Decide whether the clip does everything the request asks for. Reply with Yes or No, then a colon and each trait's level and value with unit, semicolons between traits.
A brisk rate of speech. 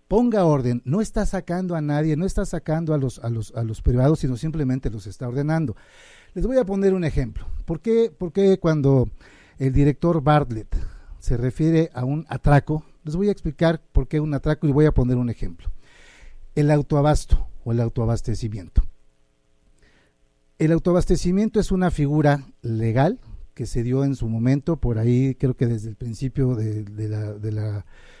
No: average, 175 wpm